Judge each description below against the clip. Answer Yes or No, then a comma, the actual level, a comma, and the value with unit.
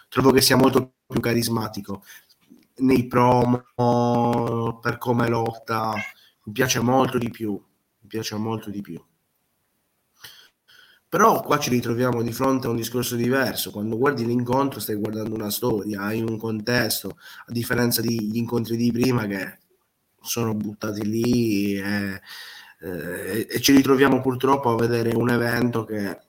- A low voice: Yes, low, 115 Hz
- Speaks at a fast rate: No, average, 145 wpm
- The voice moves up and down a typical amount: No, narrow, 2.2 semitones